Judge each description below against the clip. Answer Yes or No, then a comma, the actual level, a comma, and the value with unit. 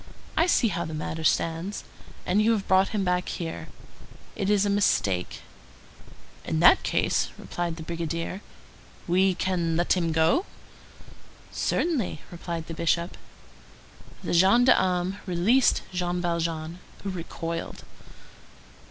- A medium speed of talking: No, slow, 125 wpm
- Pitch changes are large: No, narrow, 2.6 semitones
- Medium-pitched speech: Yes, medium, 175 Hz